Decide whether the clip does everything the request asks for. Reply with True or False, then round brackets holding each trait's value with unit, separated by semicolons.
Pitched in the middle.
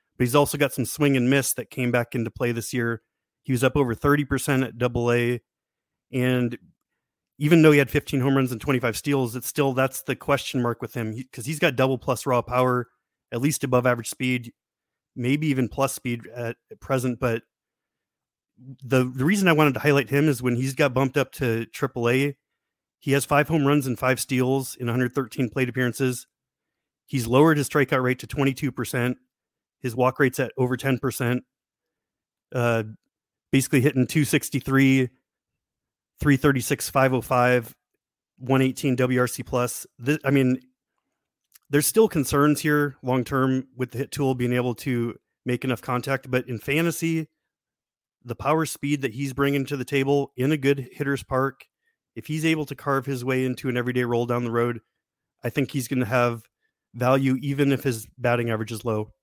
False (130 Hz)